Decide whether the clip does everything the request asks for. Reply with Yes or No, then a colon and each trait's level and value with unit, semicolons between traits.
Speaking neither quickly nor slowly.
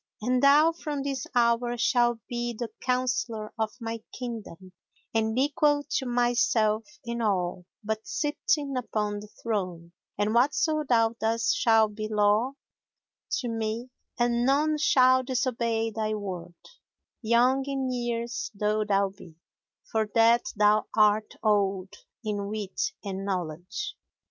No: slow, 130 wpm